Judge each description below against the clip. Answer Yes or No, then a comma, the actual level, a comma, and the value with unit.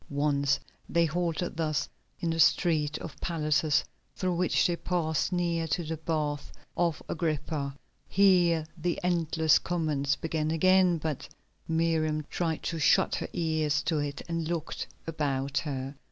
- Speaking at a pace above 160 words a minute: No, average, 140 wpm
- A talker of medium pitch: Yes, medium, 160 Hz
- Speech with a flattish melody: Yes, narrow, 2.2 semitones